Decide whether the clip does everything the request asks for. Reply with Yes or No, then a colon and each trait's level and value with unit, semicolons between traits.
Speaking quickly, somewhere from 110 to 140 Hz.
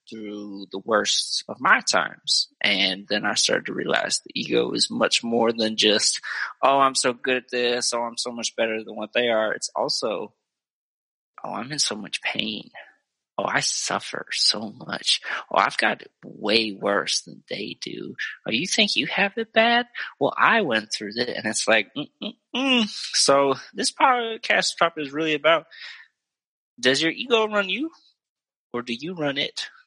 No: average, 175 wpm; low, 135 Hz